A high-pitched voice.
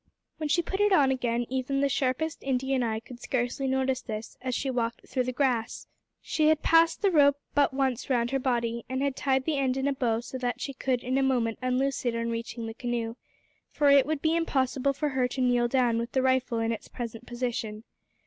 Yes: very high, 260 Hz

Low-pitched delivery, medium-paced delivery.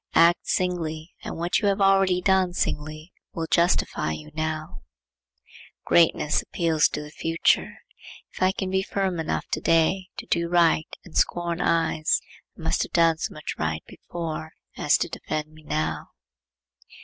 No: medium, 165 Hz; average, 160 wpm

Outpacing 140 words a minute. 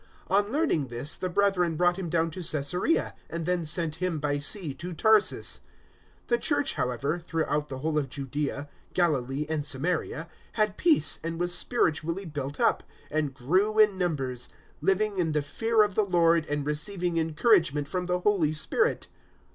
Yes: average, 170 wpm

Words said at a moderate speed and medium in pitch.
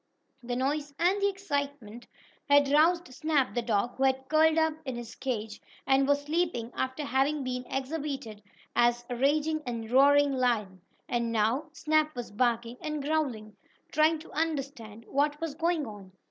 No: average, 160 wpm; very high, 275 Hz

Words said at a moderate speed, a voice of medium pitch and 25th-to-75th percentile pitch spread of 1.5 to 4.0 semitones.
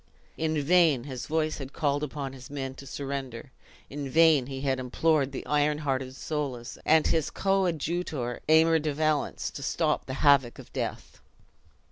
Yes: average, 160 wpm; medium, 145 Hz; average, 2.9 semitones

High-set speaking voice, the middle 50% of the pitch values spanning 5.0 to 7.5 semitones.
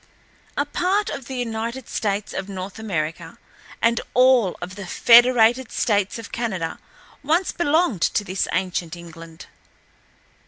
Yes: high, 220 Hz; wide, 5.5 semitones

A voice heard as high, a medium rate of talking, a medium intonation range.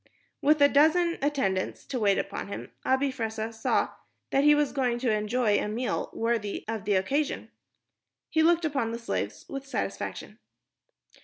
Yes: very high, 250 Hz; average, 160 wpm; average, 4.8 semitones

